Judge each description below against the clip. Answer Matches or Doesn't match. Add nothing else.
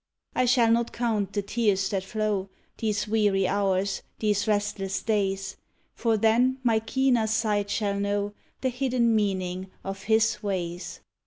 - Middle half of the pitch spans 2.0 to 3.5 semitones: Matches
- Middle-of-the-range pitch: Doesn't match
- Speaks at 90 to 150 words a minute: Matches